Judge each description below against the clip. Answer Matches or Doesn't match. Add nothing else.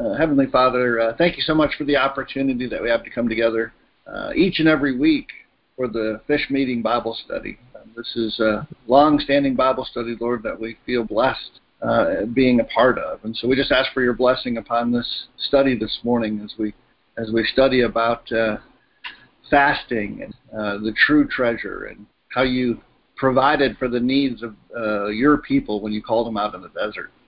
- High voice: Doesn't match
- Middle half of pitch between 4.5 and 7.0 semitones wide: Doesn't match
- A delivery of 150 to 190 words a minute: Doesn't match